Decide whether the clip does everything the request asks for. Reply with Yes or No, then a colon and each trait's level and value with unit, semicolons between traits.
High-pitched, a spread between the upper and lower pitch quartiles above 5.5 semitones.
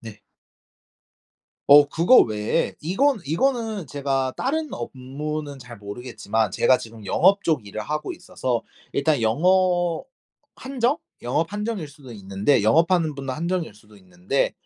No: medium, 145 Hz; wide, 7.4 semitones